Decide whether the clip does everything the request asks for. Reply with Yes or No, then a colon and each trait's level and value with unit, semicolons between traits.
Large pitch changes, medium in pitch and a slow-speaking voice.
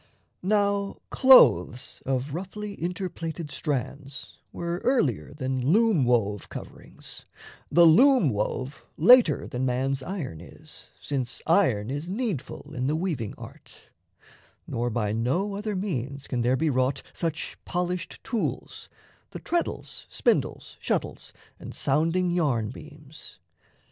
Yes: wide, 6.2 semitones; medium, 150 Hz; slow, 125 wpm